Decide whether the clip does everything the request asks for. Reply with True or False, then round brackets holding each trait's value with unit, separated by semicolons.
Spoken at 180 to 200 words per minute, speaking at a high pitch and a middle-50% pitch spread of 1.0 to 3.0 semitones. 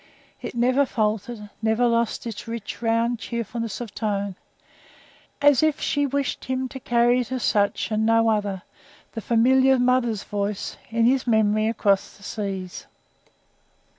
False (145 wpm; 230 Hz; 2.7 semitones)